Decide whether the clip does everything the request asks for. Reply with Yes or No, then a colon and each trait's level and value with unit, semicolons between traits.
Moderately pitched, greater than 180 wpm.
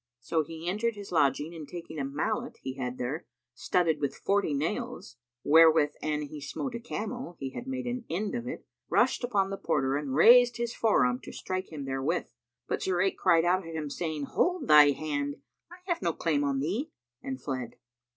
Yes: medium, 165 Hz; average, 195 wpm